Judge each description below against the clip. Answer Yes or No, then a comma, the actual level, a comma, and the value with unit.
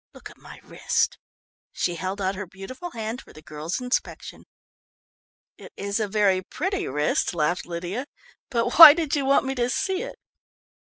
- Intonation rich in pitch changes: Yes, wide, 6.4 semitones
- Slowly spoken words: No, average, 170 wpm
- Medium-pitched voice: No, high, 215 Hz